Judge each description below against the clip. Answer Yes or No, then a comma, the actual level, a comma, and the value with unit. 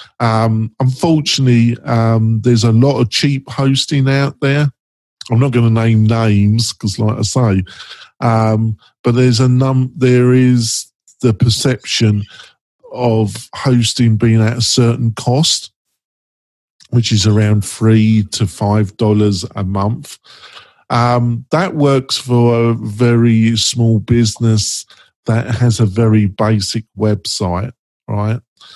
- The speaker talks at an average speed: No, slow, 125 wpm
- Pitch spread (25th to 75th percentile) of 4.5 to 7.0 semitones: No, narrow, 2.5 semitones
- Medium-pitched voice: No, low, 115 Hz